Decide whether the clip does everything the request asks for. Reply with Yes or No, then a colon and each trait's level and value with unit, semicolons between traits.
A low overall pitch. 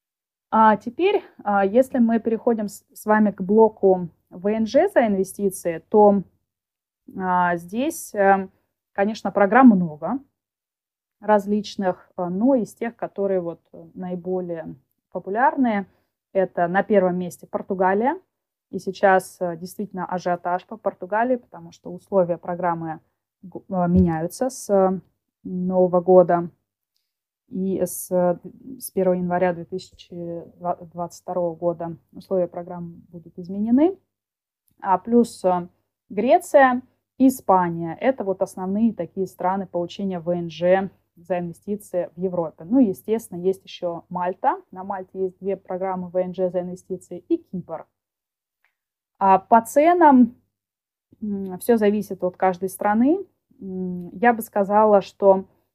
No: high, 190 Hz